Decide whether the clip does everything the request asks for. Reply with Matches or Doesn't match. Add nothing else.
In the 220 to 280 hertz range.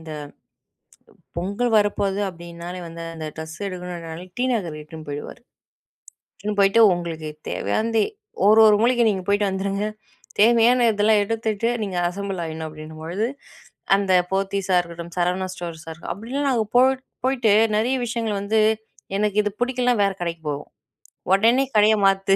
Doesn't match